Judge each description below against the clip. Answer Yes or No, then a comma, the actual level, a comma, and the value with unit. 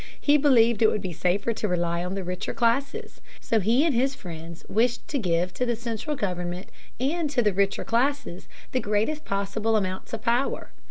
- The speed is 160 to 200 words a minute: Yes, average, 195 wpm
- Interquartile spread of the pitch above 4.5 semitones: Yes, average, 5.3 semitones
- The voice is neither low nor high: No, high, 220 Hz